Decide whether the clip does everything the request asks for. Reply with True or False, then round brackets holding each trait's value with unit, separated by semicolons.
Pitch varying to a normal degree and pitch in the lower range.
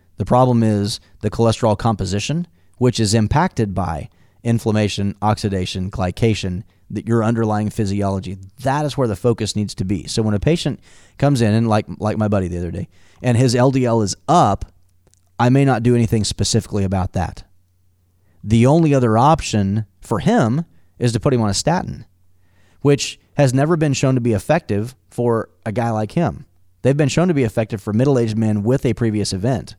True (4.0 semitones; 110 Hz)